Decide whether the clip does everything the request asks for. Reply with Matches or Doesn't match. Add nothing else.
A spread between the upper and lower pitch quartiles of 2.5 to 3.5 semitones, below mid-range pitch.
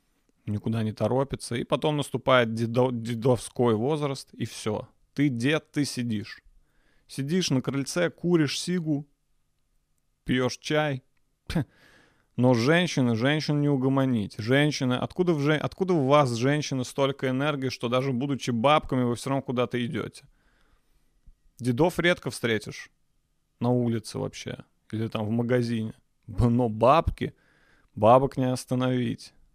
Matches